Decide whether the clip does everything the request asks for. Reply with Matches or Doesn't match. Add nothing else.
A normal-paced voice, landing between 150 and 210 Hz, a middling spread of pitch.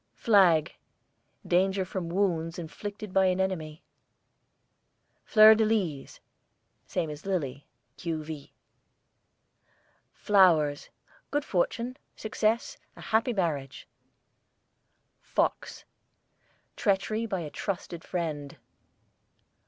Doesn't match